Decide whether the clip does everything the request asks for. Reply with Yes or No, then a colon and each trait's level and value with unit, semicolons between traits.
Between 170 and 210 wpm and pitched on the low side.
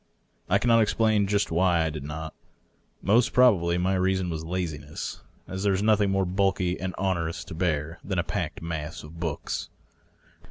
Yes: average, 175 wpm; very low, 90 Hz